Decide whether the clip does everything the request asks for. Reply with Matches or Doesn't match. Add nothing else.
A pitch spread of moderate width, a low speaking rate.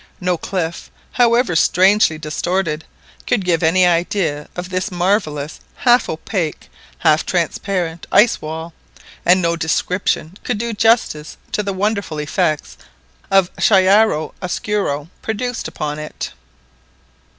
Matches